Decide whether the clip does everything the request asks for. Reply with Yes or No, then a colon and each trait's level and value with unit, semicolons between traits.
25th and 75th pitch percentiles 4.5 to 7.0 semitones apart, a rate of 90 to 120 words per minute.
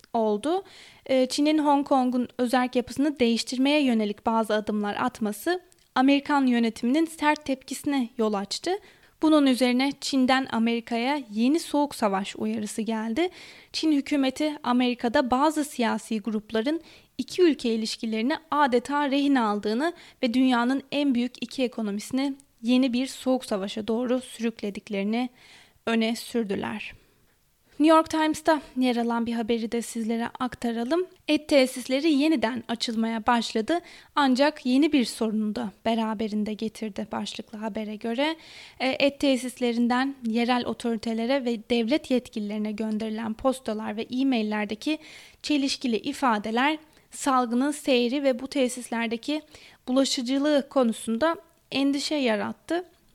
No: average, 4.0 semitones; average, 110 wpm